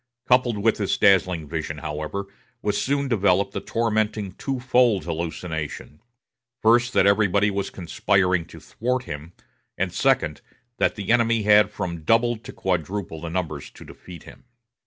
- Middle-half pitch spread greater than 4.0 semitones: Yes, average, 5.1 semitones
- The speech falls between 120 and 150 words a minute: Yes, average, 140 wpm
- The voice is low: Yes, low, 100 Hz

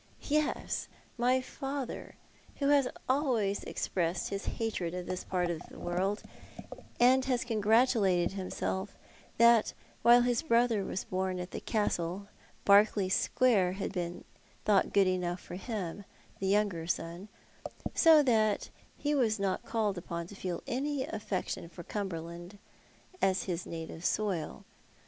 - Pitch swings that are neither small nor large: Yes, average, 4.7 semitones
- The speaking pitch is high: Yes, high, 200 Hz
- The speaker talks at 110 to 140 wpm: Yes, slow, 135 wpm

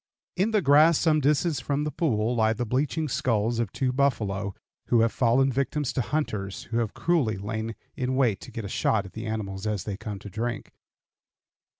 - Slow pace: No, average, 200 wpm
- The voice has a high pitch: No, low, 120 Hz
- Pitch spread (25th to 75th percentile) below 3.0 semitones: No, average, 4.6 semitones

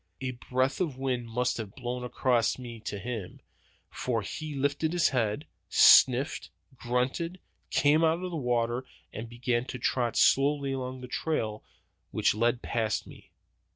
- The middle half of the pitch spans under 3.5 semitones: Yes, average, 2.8 semitones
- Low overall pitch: Yes, low, 125 Hz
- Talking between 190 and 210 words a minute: No, average, 155 wpm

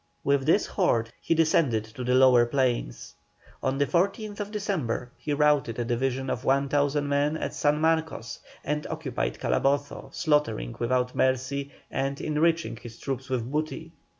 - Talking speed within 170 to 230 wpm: No, average, 150 wpm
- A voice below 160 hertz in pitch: Yes, medium, 140 Hz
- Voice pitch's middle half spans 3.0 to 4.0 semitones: Yes, average, 3.6 semitones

